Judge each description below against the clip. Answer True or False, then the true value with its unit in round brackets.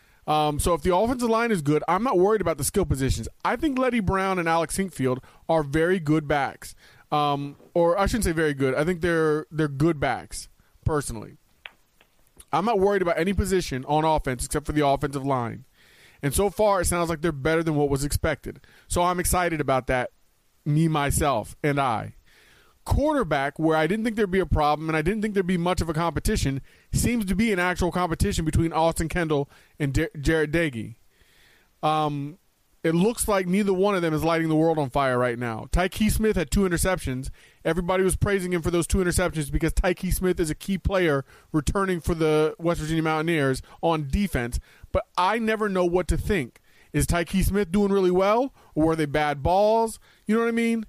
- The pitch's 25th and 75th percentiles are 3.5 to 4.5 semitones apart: True (4.2 semitones)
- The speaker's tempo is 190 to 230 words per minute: True (205 wpm)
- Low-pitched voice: False (165 Hz)